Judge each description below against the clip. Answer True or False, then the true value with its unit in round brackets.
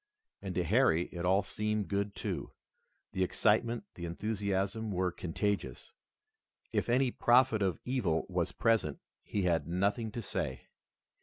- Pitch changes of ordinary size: True (3.7 semitones)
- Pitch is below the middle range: True (100 Hz)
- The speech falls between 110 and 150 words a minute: True (140 wpm)